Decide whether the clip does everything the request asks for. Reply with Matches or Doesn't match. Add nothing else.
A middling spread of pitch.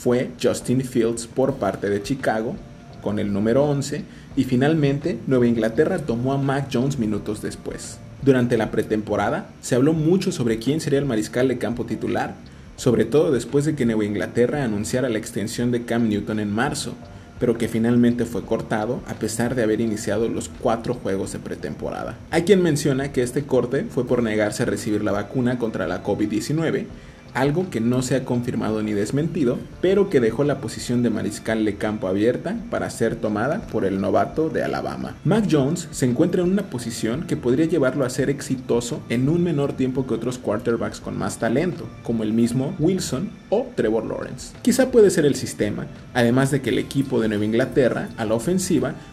Matches